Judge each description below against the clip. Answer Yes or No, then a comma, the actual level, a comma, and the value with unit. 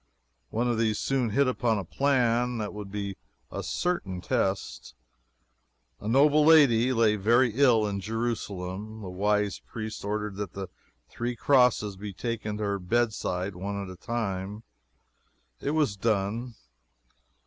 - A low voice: Yes, low, 110 Hz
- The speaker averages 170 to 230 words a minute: No, average, 145 wpm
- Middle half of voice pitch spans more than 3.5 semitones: No, average, 3.2 semitones